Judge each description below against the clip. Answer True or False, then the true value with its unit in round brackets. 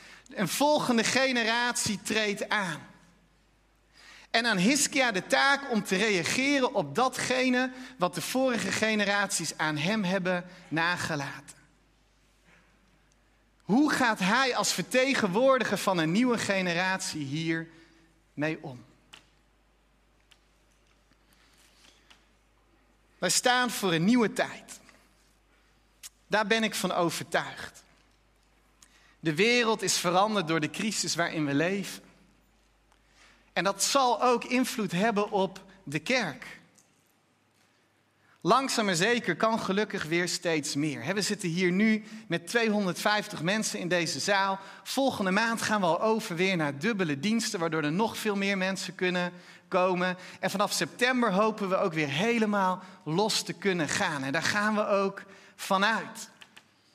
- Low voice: False (195 Hz)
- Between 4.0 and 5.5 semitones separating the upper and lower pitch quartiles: True (4.5 semitones)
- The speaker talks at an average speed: False (125 wpm)